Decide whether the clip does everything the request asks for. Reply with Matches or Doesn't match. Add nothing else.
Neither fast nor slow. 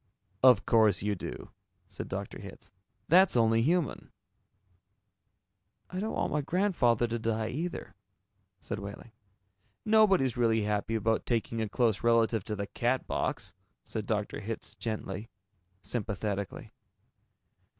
Doesn't match